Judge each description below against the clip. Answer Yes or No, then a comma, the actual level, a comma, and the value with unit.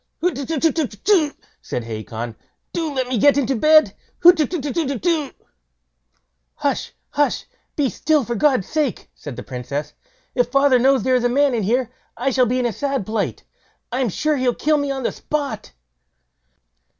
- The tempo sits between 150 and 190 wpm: Yes, average, 155 wpm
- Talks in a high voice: Yes, very high, 265 Hz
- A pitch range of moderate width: Yes, average, 4.0 semitones